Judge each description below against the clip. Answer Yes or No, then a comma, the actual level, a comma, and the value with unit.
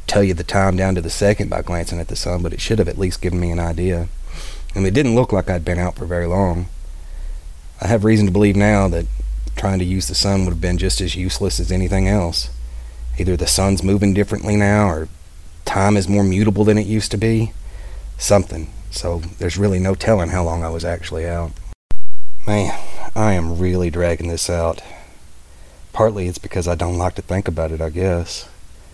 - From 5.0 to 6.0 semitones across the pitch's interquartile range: No, average, 3.0 semitones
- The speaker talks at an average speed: No, fast, 215 wpm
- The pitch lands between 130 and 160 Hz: No, very low, 90 Hz